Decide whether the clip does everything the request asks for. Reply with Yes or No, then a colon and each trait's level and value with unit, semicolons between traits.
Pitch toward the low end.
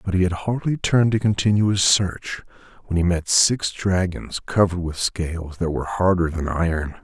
Yes: very low, 90 Hz